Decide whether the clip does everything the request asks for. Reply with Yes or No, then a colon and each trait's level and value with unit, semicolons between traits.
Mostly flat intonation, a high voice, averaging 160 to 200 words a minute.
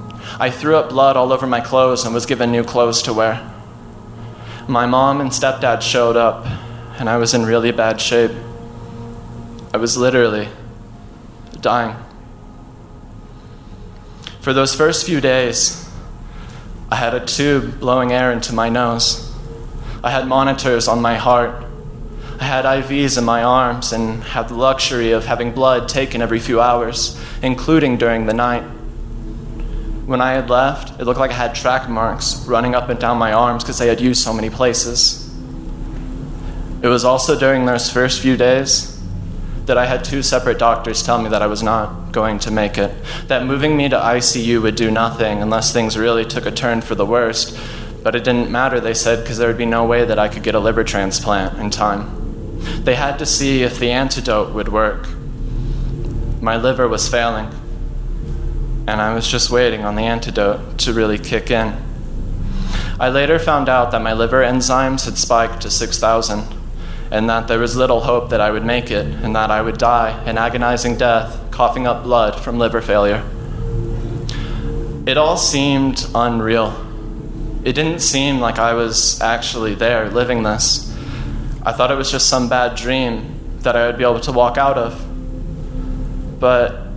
No: narrow, 2.0 semitones; low, 120 Hz; average, 175 wpm